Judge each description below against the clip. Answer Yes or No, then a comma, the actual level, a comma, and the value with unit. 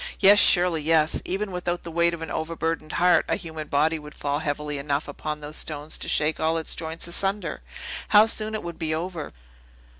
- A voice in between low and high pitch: Yes, medium, 160 Hz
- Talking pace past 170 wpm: Yes, average, 200 wpm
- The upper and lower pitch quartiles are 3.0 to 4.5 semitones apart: No, narrow, 2.5 semitones